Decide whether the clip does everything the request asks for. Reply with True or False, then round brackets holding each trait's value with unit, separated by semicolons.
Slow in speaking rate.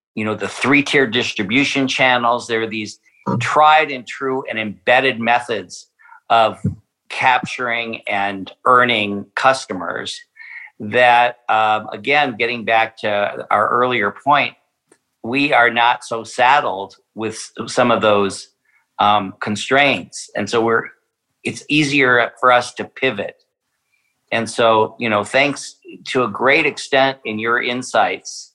True (130 wpm)